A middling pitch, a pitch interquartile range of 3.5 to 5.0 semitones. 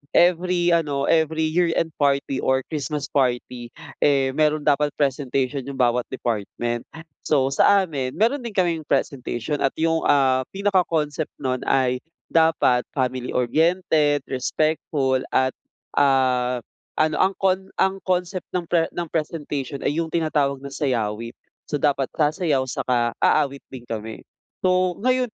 Yes: medium, 145 Hz; average, 4.0 semitones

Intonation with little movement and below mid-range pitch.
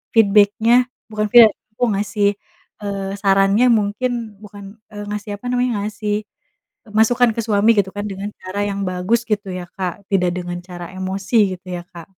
No: narrow, 1.9 semitones; high, 205 Hz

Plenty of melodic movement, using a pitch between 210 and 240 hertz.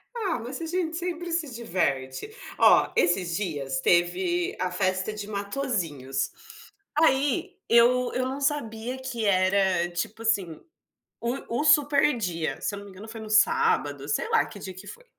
Yes: wide, 8.0 semitones; high, 225 Hz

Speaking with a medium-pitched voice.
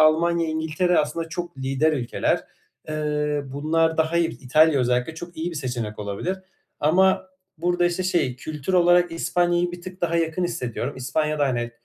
Yes: medium, 160 Hz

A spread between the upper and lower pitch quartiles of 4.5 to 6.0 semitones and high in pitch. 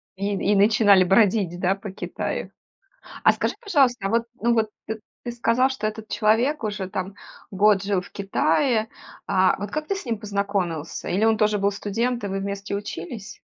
No: average, 2.7 semitones; high, 210 Hz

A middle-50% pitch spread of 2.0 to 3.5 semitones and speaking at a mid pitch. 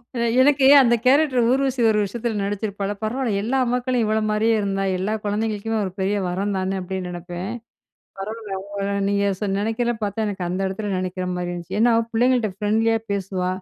No: average, 3.2 semitones; high, 205 Hz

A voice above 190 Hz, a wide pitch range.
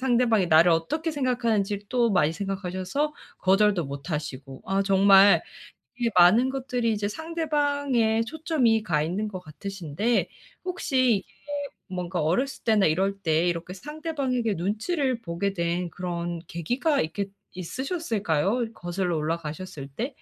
Yes: high, 200 Hz; wide, 6.3 semitones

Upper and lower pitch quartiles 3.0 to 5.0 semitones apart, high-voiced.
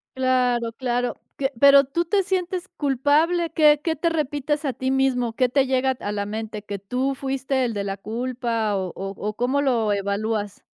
Yes: average, 4.2 semitones; very high, 255 Hz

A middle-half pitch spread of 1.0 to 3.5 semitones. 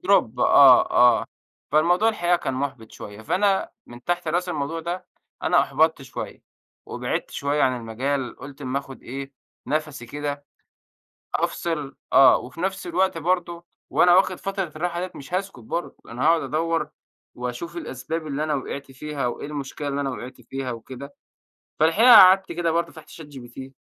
No: average, 4.5 semitones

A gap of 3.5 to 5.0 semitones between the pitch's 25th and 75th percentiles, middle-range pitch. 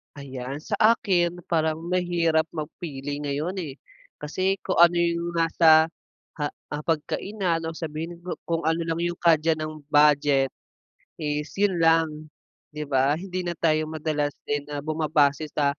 No: narrow, 2.4 semitones; medium, 160 Hz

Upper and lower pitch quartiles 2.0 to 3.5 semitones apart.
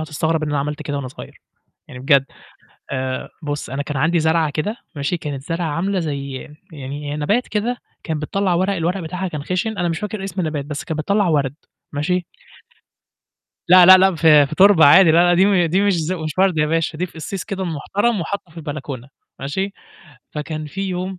No: average, 4.0 semitones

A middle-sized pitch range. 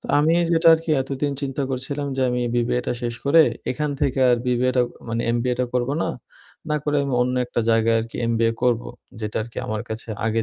Yes: average, 3.2 semitones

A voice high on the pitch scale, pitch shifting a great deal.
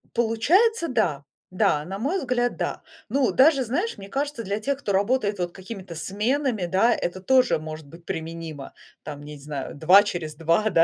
Yes: high, 200 Hz; wide, 7.3 semitones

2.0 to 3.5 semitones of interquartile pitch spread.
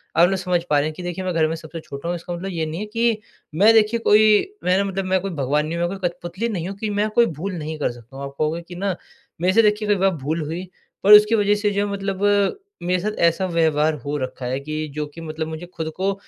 No: average, 4.0 semitones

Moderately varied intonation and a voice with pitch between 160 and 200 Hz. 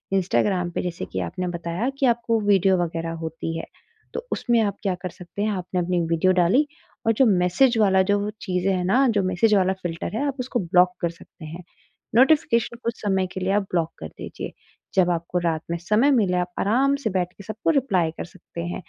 Yes: average, 4.2 semitones; medium, 185 Hz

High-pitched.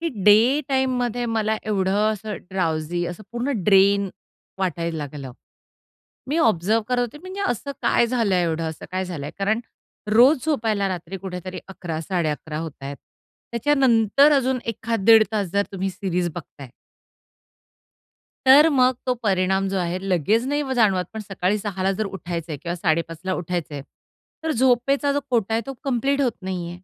Yes: high, 200 Hz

